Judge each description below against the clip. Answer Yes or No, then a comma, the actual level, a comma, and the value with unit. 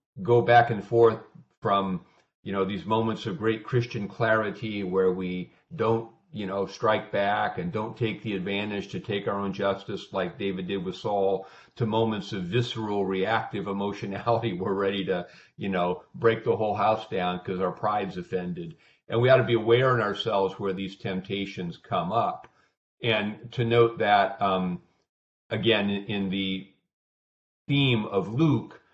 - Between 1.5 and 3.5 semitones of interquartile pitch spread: Yes, average, 3.0 semitones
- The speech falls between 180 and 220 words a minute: No, average, 165 wpm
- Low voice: Yes, low, 100 Hz